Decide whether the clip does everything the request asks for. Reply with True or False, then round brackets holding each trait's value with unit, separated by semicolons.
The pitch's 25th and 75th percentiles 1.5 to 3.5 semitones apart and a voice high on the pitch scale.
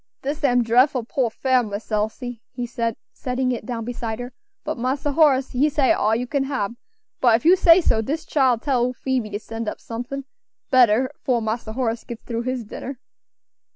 True (2.8 semitones; 245 Hz)